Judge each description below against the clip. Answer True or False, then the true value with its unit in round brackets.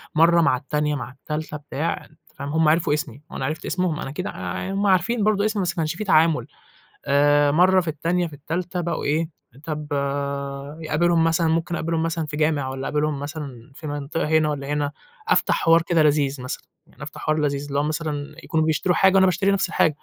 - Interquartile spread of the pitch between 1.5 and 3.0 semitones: True (2.7 semitones)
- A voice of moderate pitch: True (155 Hz)